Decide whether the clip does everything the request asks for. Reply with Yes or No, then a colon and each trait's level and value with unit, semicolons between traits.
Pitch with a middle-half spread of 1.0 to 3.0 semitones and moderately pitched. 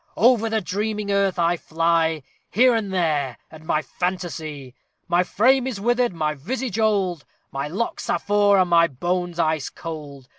No: average, 5.0 semitones; medium, 175 Hz